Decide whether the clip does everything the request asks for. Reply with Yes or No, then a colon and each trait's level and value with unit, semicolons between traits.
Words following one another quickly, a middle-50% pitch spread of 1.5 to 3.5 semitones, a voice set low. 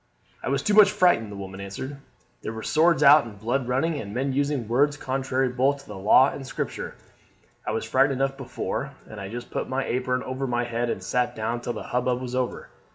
Yes: fast, 225 wpm; narrow, 2.6 semitones; low, 130 Hz